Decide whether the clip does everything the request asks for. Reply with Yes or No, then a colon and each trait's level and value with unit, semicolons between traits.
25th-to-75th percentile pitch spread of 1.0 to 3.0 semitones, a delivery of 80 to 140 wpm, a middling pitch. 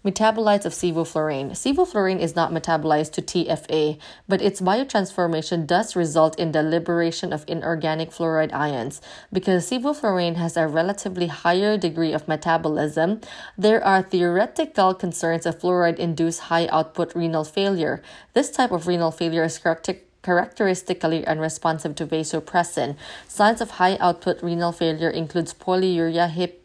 Yes: narrow, 2.5 semitones; slow, 135 wpm; medium, 170 Hz